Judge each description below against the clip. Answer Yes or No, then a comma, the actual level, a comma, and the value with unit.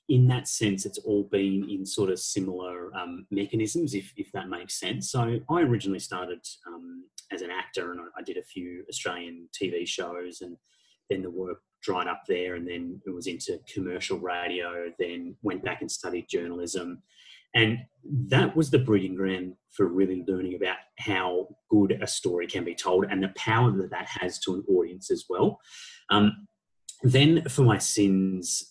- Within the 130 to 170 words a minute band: No, average, 180 wpm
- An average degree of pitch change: No, wide, 7.5 semitones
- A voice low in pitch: Yes, low, 100 Hz